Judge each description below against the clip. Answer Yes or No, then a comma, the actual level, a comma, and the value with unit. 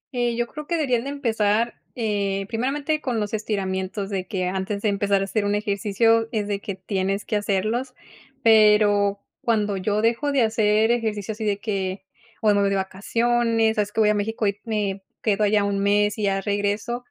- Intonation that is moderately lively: No, narrow, 2.2 semitones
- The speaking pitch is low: No, high, 210 Hz